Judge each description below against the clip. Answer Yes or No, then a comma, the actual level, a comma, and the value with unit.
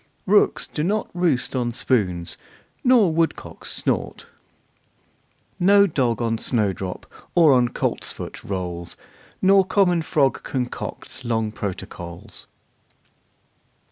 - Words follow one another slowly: Yes, slow, 100 wpm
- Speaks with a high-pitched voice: No, low, 125 Hz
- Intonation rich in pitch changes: Yes, wide, 8.7 semitones